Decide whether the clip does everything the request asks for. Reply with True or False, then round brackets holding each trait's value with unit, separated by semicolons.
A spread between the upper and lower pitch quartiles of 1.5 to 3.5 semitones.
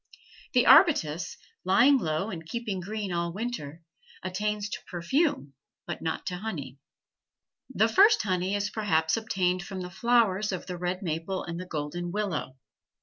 False (3.9 semitones)